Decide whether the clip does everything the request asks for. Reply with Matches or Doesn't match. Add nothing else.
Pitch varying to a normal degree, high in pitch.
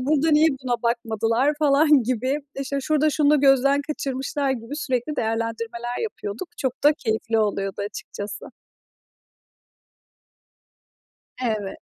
Matches